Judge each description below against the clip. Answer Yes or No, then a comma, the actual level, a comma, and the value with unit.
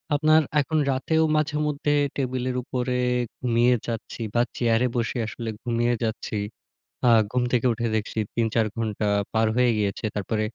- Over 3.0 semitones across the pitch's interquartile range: No, narrow, 2.4 semitones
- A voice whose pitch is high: No, low, 120 Hz